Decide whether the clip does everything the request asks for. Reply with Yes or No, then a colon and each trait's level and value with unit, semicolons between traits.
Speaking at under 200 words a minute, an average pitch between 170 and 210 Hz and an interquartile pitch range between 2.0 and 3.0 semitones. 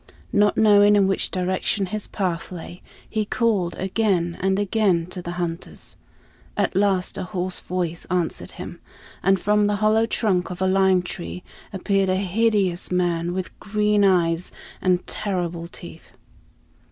Yes: average, 150 wpm; medium, 185 Hz; narrow, 2.5 semitones